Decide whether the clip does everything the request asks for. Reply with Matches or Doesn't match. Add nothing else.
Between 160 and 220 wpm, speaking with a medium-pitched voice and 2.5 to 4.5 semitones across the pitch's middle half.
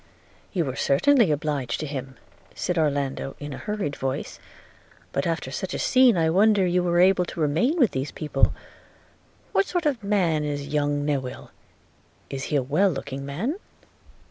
Doesn't match